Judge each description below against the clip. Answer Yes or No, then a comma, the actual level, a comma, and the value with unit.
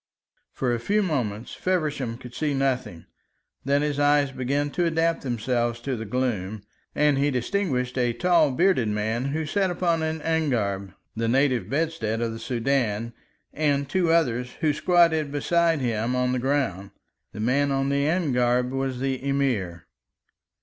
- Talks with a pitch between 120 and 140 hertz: Yes, low, 135 Hz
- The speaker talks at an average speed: Yes, average, 155 wpm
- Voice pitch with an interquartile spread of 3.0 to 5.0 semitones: Yes, average, 4.3 semitones